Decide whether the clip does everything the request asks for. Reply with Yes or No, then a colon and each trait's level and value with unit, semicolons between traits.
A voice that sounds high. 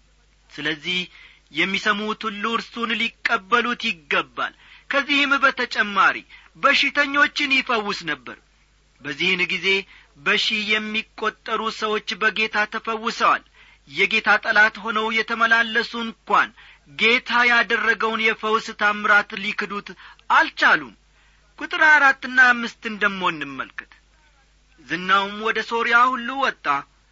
Yes: high, 220 Hz